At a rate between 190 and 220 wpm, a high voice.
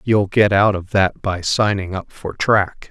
No: fast, 205 wpm; low, 100 Hz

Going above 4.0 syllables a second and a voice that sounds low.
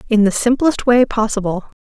No: 5.1 syllables/s; high, 225 Hz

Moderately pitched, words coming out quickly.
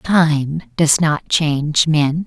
No: medium, 155 Hz; slow, 135 wpm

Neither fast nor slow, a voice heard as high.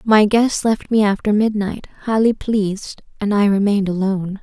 Yes: average, 165 wpm; high, 205 Hz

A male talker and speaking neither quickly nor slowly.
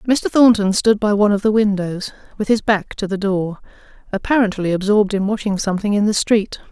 No: female; average, 195 wpm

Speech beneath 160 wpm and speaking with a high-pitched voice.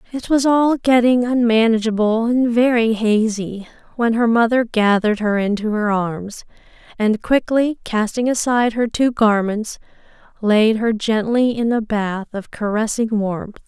Yes: average, 140 wpm; high, 225 Hz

